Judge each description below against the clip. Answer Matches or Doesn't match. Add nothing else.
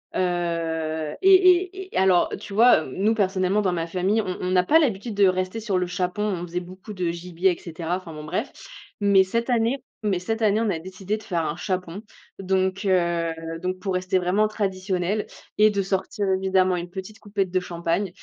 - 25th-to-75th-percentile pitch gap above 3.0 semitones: Doesn't match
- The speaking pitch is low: Doesn't match